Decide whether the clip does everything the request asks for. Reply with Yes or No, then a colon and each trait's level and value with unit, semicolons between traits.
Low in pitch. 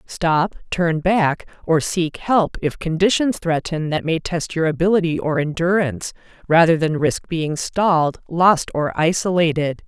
No: medium, 165 Hz